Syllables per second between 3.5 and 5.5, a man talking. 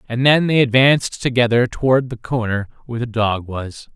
Yes: 5.3 syllables/s; male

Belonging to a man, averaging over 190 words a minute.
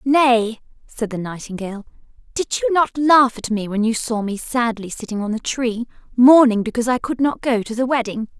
No: female; average, 200 wpm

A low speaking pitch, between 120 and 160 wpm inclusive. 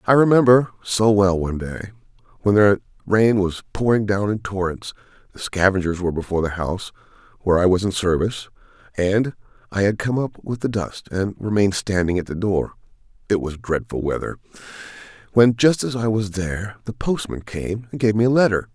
No: low, 105 Hz; average, 175 wpm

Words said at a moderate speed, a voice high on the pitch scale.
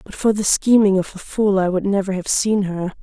No: fast, 260 wpm; high, 195 Hz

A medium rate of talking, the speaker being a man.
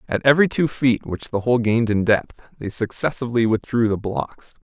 Yes: average, 195 wpm; male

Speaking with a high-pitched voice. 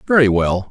No: low, 115 Hz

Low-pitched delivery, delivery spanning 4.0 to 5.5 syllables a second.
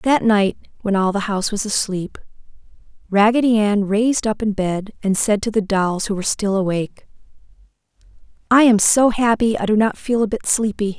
No: high, 210 Hz; 5.3 syllables/s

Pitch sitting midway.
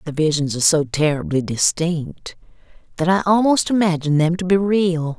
Yes: medium, 165 Hz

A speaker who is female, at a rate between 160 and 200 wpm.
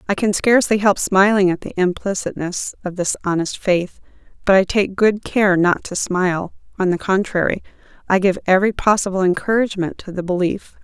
Yes: female; average, 170 wpm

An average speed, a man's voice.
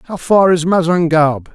Yes: average, 155 wpm; male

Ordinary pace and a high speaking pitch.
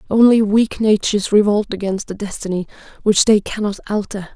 Yes: average, 150 wpm; high, 205 Hz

